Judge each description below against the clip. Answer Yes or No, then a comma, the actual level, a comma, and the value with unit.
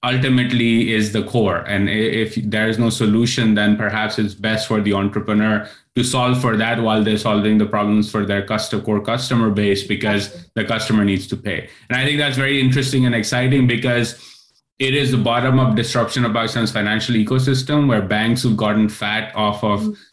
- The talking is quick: No, average, 185 wpm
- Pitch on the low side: Yes, low, 110 Hz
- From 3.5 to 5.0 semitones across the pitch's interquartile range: No, narrow, 2.6 semitones